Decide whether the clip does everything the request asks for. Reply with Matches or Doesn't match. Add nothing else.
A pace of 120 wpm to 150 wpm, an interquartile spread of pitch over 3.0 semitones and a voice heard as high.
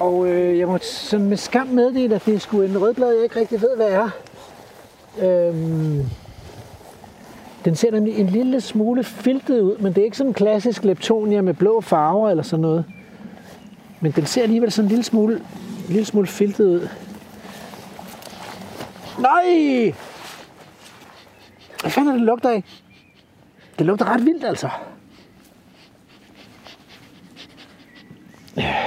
Matches